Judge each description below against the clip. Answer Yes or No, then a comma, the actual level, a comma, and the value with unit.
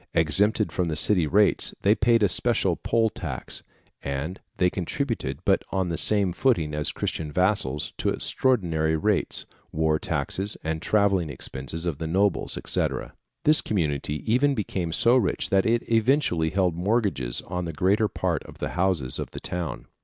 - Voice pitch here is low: Yes, very low, 90 Hz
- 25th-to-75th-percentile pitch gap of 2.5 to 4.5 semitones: No, average, 5.0 semitones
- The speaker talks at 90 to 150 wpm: No, average, 165 wpm